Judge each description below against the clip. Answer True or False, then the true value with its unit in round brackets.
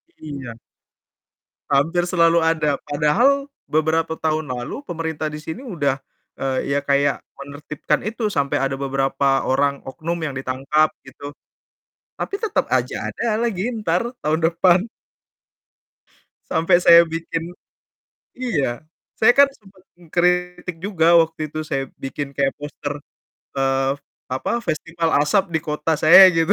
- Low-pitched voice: False (160 Hz)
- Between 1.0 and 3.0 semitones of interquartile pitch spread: False (3.7 semitones)